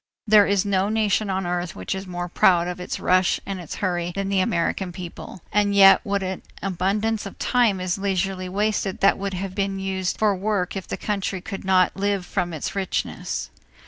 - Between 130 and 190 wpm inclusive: No, fast, 205 wpm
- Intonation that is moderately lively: No, narrow, 1.7 semitones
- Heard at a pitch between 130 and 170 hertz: No, high, 190 Hz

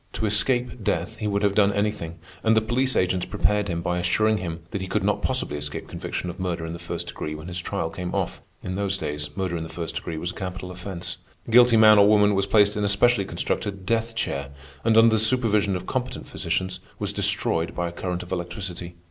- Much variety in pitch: No, average, 3.3 semitones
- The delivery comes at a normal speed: No, fast, 230 wpm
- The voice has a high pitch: No, very low, 95 Hz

